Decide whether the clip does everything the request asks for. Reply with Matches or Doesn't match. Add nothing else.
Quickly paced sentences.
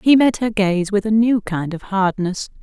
Matches